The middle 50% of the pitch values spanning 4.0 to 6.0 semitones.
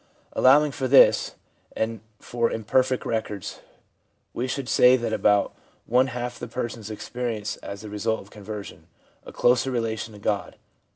No: average, 2.7 semitones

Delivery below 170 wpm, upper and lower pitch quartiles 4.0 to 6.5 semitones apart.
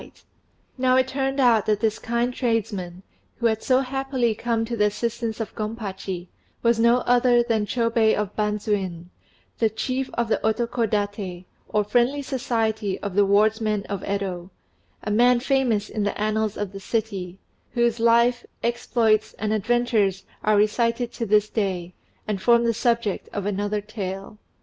No: average, 160 wpm; narrow, 2.6 semitones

